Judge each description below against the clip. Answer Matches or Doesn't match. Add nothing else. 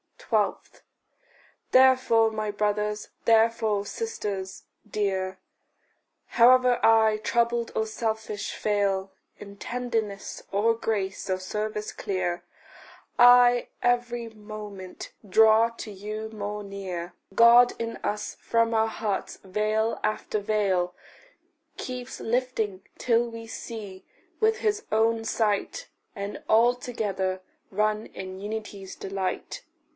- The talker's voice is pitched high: Matches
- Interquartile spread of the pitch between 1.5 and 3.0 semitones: Matches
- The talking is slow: Matches